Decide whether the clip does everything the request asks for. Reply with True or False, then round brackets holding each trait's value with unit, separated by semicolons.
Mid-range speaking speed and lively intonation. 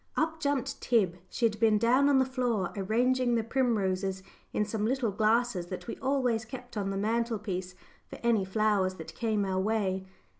False (180 wpm; 4.0 semitones)